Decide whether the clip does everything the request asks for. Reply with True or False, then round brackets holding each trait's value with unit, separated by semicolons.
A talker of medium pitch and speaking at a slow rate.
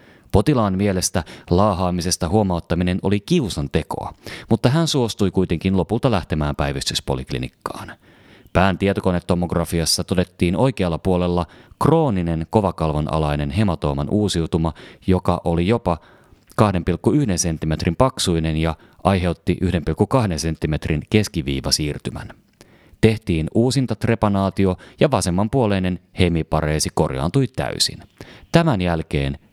False (90 Hz; 90 wpm)